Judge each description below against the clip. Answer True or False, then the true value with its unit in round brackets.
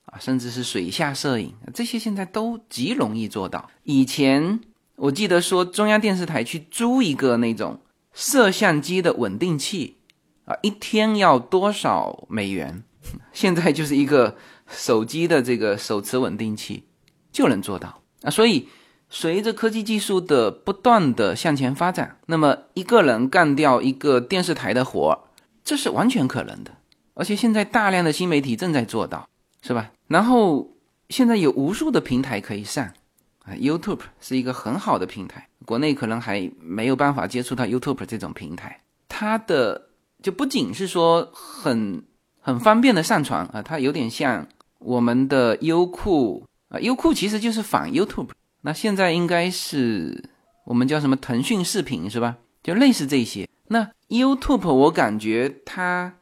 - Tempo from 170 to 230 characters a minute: False (265 characters per minute)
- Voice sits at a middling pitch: True (165 Hz)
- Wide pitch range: True (8.8 semitones)